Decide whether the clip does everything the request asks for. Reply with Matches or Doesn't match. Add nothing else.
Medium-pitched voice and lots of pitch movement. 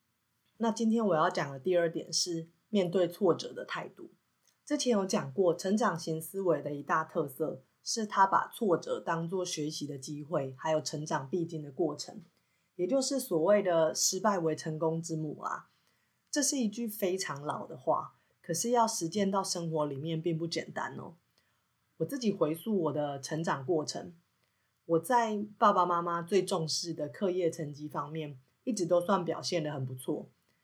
Doesn't match